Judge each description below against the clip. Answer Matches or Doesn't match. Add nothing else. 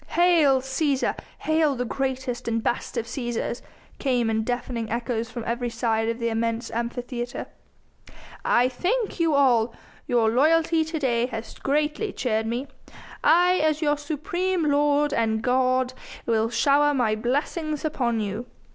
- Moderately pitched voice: Doesn't match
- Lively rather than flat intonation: Doesn't match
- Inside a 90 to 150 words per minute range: Matches